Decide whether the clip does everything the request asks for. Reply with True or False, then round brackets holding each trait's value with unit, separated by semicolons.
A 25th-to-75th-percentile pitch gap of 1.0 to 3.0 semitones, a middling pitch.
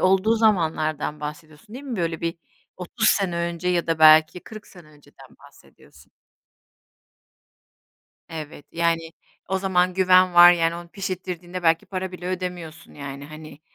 True (2.7 semitones; 175 Hz)